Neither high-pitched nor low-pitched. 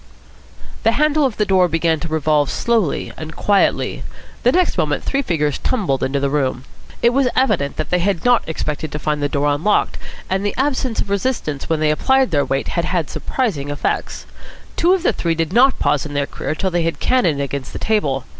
Yes: medium, 170 Hz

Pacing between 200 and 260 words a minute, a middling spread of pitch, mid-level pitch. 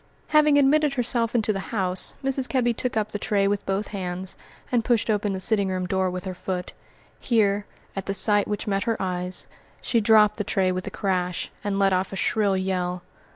No: fast, 205 wpm; average, 3.0 semitones; high, 200 Hz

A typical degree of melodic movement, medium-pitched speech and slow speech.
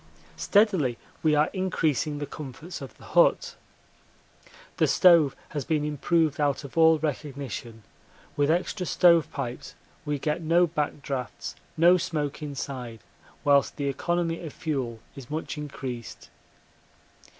Yes: average, 3.1 semitones; medium, 150 Hz; slow, 130 wpm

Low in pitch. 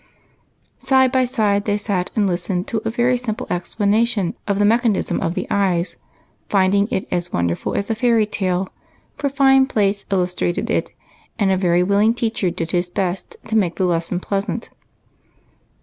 No: high, 200 Hz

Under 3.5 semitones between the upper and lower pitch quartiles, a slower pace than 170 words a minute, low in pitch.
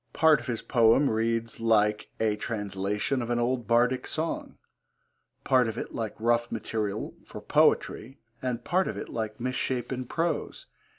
Yes: average, 2.7 semitones; average, 155 wpm; low, 115 Hz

